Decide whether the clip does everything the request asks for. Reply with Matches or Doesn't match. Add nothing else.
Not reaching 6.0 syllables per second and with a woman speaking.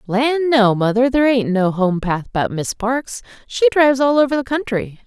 Matches